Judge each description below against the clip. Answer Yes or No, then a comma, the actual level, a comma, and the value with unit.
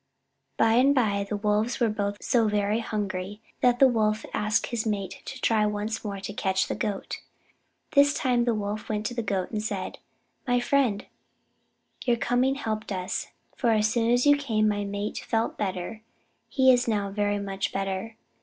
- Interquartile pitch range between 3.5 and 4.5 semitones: No, average, 2.8 semitones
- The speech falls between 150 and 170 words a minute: No, average, 180 wpm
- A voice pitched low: No, high, 215 Hz